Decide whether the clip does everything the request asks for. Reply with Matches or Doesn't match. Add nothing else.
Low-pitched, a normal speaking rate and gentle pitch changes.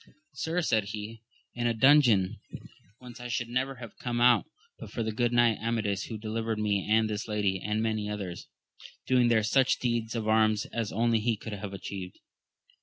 Matches